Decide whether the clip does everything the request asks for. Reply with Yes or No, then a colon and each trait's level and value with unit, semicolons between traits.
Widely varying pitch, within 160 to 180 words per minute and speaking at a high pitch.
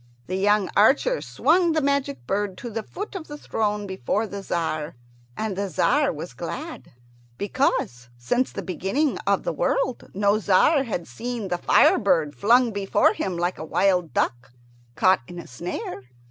Yes: wide, 5.8 semitones; average, 170 wpm; high, 200 Hz